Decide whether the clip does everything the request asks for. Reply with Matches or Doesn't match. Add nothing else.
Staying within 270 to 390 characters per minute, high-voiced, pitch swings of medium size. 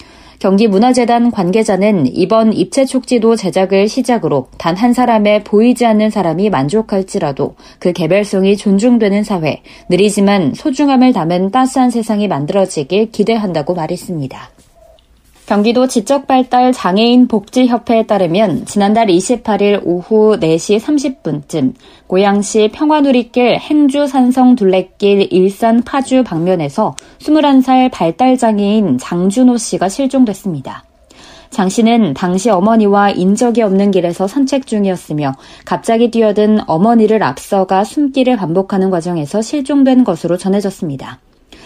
Matches